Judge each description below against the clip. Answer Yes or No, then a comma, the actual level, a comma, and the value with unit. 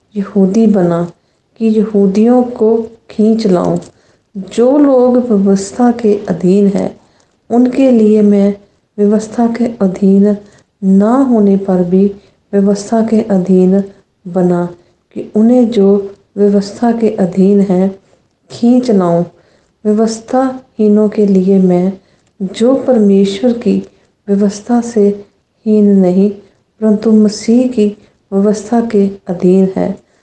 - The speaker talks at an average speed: No, slow, 105 wpm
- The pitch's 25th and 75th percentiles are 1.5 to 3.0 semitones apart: Yes, narrow, 2.4 semitones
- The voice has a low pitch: No, high, 205 Hz